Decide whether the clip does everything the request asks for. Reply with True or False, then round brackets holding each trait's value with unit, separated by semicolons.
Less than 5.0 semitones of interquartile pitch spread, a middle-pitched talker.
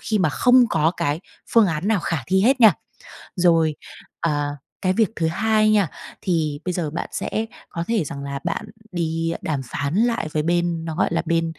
True (4.4 semitones; 170 Hz)